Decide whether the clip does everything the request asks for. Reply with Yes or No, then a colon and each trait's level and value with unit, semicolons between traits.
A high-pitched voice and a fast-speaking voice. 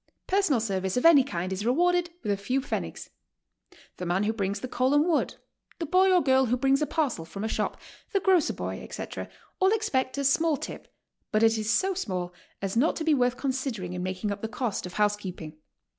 Yes: very high, 250 Hz; fast, 215 wpm